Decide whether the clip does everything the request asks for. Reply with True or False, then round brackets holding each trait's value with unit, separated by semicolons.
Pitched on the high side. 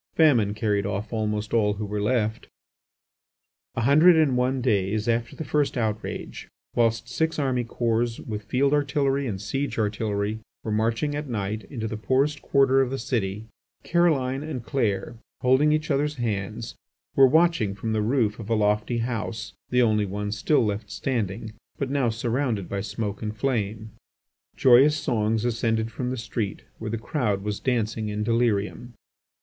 False (115 Hz)